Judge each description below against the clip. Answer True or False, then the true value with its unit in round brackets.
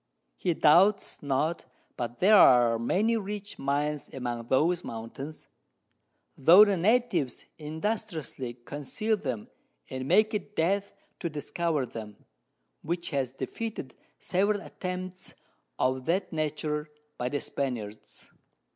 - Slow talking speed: True (115 wpm)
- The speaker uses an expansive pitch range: True (6.5 semitones)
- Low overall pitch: False (155 Hz)